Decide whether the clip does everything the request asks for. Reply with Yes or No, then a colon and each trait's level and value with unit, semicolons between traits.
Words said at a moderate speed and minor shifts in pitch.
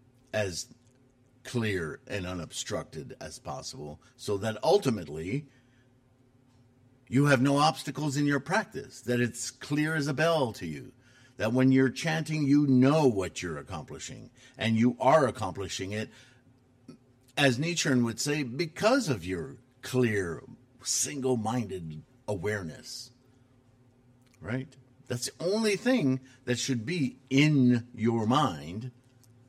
No: slow, 120 wpm; narrow, 1.7 semitones